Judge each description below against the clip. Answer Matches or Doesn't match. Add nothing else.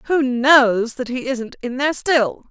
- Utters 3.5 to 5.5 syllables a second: Matches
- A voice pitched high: Matches